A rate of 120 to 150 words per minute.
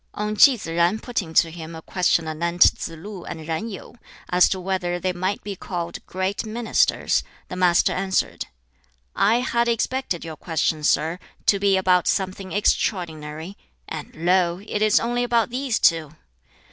No: average, 165 wpm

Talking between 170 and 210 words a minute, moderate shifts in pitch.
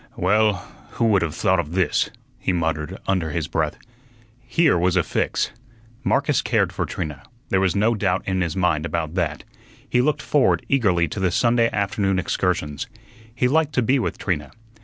Yes: average, 180 wpm; average, 4.4 semitones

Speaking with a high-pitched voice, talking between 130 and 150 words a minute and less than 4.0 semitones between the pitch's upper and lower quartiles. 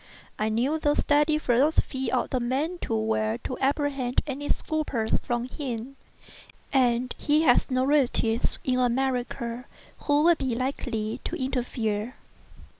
Yes: very high, 255 Hz; slow, 135 wpm; average, 3.4 semitones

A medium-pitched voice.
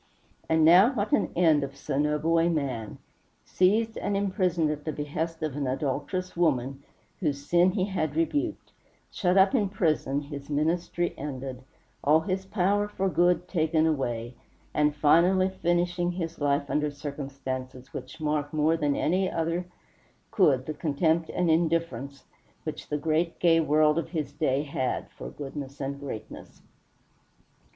Yes: medium, 155 Hz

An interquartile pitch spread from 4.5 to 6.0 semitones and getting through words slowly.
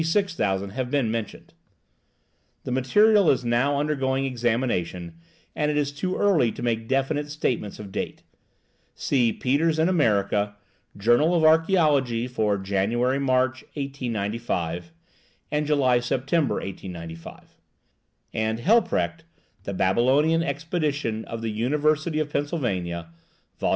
Yes: average, 5.3 semitones; slow, 120 wpm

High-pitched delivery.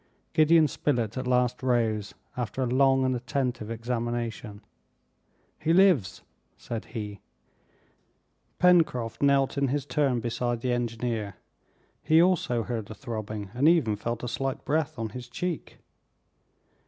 No: low, 125 Hz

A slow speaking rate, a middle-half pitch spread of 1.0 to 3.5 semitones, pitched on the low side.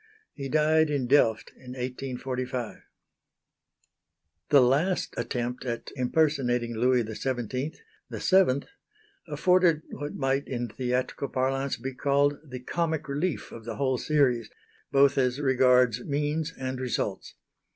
Yes: slow, 120 wpm; narrow, 2.6 semitones; low, 130 Hz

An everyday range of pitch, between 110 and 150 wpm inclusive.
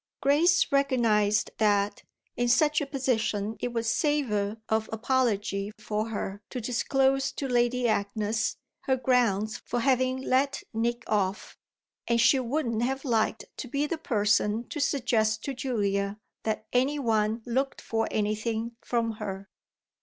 Yes: average, 3.5 semitones; average, 140 wpm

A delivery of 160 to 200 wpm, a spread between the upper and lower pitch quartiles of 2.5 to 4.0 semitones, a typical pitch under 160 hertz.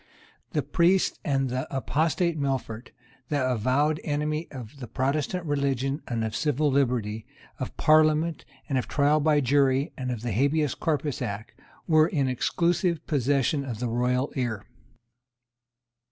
No: average, 140 wpm; average, 3.3 semitones; medium, 140 Hz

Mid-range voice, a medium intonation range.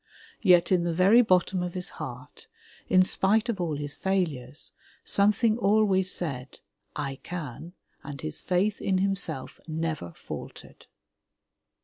Yes: medium, 180 Hz; average, 4.1 semitones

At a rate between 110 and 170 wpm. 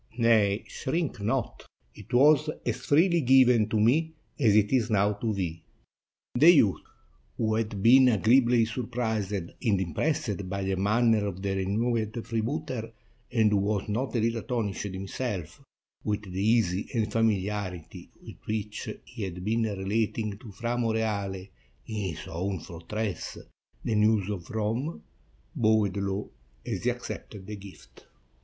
Yes: average, 145 wpm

